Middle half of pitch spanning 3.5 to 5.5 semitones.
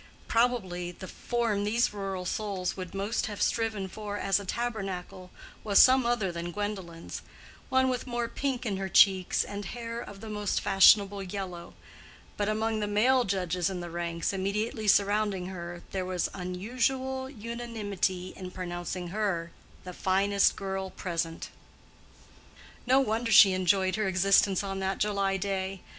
No: average, 2.8 semitones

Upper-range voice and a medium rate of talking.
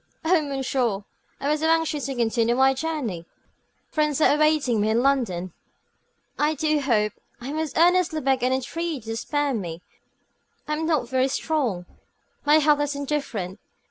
Yes: very high, 275 Hz; average, 165 wpm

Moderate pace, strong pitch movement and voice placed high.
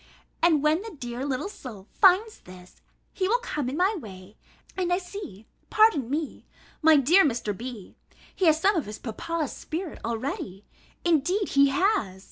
Yes: average, 165 wpm; wide, 7.9 semitones; very high, 300 Hz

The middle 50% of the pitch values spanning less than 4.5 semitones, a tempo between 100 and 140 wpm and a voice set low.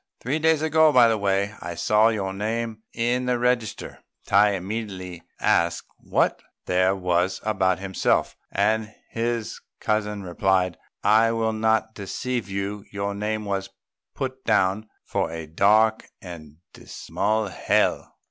Yes: average, 2.9 semitones; slow, 135 wpm; low, 105 Hz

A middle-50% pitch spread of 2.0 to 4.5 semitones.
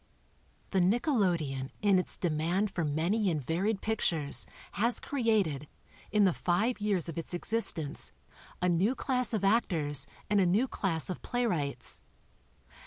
No: average, 5.2 semitones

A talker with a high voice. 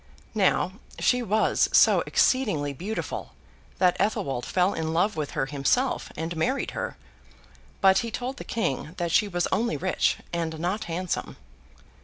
No: medium, 180 Hz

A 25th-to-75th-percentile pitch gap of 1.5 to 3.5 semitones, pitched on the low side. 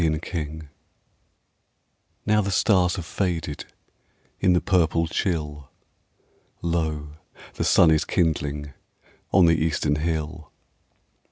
Yes: narrow, 2.6 semitones; very low, 80 Hz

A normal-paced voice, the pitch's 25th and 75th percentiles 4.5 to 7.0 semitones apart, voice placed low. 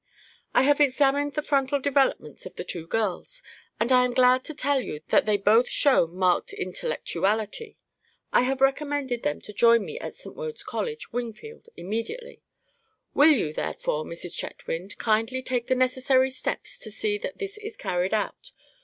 No: average, 170 wpm; average, 5.2 semitones; very high, 255 Hz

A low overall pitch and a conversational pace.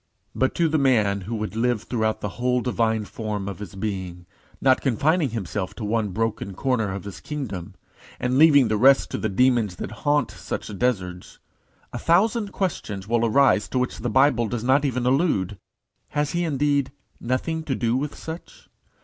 Yes: low, 120 Hz; average, 180 wpm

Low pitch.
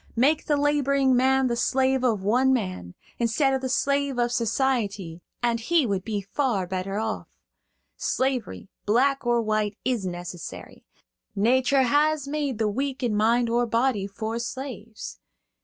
No: high, 240 Hz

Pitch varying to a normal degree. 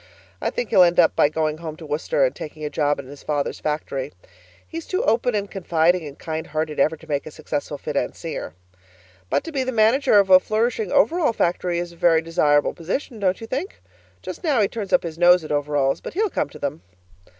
No: wide, 6.6 semitones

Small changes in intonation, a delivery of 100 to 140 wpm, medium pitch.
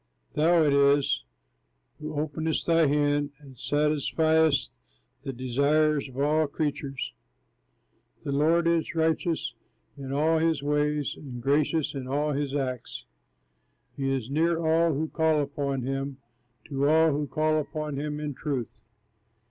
Yes: narrow, 2.1 semitones; slow, 135 wpm; medium, 150 Hz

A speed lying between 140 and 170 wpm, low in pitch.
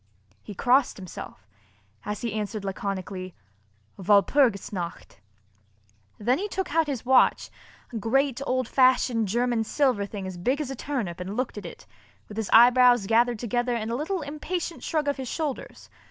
No: average, 165 wpm; high, 240 Hz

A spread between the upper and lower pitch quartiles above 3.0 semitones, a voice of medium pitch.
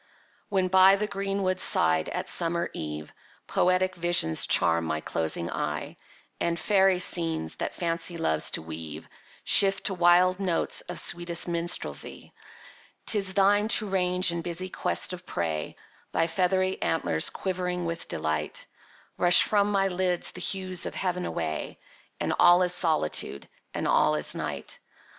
No: narrow, 2.5 semitones; medium, 175 Hz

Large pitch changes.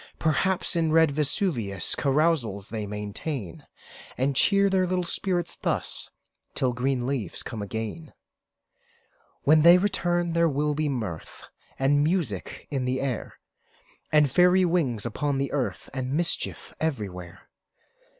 Yes: wide, 6.0 semitones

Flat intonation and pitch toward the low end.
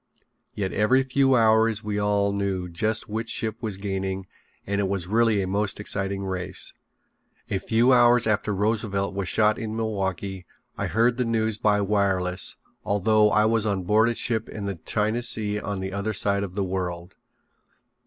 Yes: narrow, 2.3 semitones; low, 105 Hz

